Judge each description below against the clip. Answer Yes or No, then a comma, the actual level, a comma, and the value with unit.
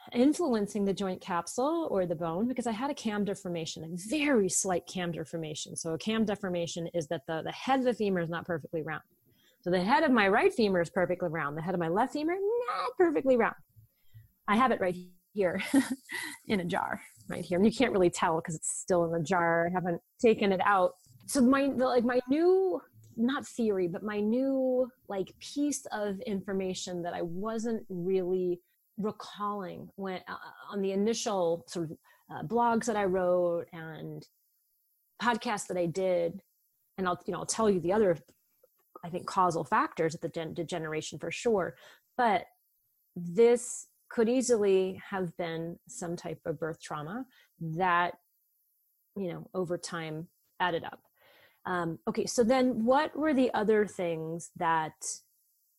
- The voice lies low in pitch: No, high, 190 Hz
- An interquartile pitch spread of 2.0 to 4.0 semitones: No, wide, 5.4 semitones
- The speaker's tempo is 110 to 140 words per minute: No, average, 175 wpm